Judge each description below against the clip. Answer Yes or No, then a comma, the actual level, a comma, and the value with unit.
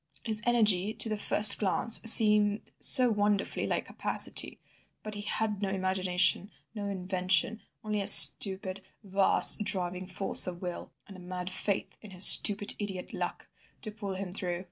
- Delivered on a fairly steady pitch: Yes, narrow, 2.2 semitones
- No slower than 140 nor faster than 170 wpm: Yes, average, 160 wpm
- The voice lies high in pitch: Yes, high, 200 Hz